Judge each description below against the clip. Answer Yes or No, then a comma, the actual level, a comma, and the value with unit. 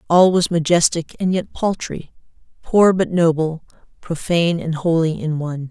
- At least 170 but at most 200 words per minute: No, average, 145 wpm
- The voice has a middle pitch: Yes, medium, 165 Hz